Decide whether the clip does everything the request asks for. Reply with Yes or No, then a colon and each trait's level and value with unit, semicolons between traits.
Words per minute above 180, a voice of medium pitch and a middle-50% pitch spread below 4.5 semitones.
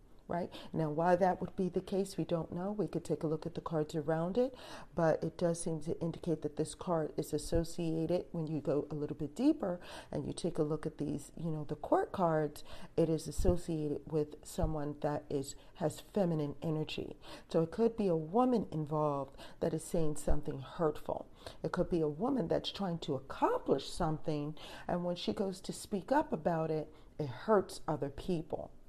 Yes: average, 200 wpm; medium, 160 Hz; average, 2.8 semitones